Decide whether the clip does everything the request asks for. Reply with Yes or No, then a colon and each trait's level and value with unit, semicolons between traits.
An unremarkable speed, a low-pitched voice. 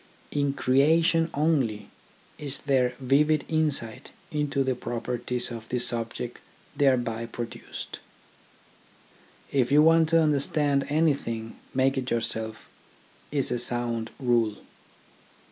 No: slow, 110 wpm; low, 130 Hz